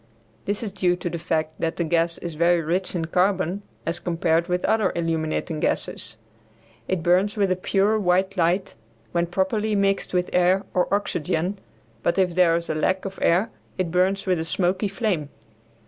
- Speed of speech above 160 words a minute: Yes, average, 180 wpm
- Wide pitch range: No, narrow, 2.4 semitones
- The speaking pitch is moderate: Yes, medium, 180 Hz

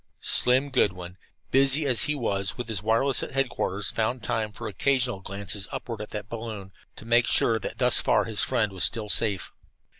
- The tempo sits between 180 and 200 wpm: Yes, average, 185 wpm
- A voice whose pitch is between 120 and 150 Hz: No, low, 110 Hz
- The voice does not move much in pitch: No, average, 3.8 semitones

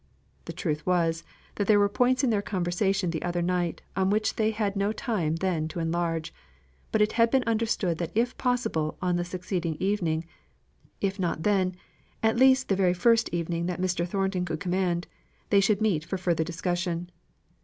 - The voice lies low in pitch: No, medium, 185 Hz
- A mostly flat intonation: No, average, 3.4 semitones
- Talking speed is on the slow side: No, average, 185 wpm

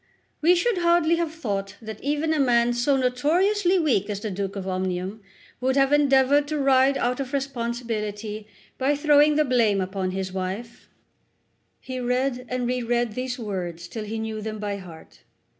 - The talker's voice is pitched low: No, high, 245 Hz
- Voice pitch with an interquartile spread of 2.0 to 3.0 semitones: No, average, 5.3 semitones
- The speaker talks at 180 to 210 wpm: No, average, 170 wpm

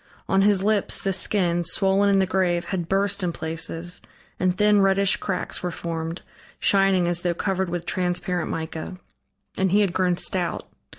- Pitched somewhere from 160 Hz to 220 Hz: Yes, medium, 185 Hz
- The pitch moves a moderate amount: No, narrow, 2.0 semitones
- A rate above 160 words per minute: Yes, average, 170 wpm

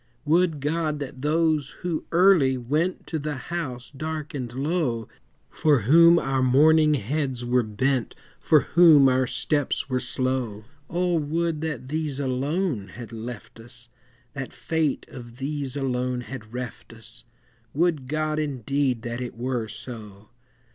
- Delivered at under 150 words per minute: Yes, average, 140 wpm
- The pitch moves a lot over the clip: No, average, 3.9 semitones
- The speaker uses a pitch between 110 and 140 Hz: Yes, low, 135 Hz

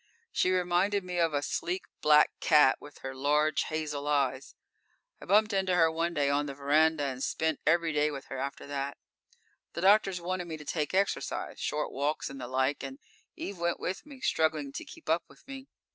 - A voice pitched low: No, medium, 155 Hz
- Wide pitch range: No, average, 3.9 semitones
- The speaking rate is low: No, average, 200 wpm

